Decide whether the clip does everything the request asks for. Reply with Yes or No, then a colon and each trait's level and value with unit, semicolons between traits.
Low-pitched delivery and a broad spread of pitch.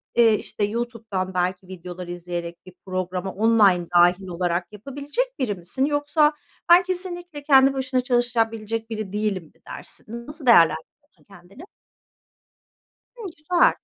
No: high, 220 Hz; wide, 6.9 semitones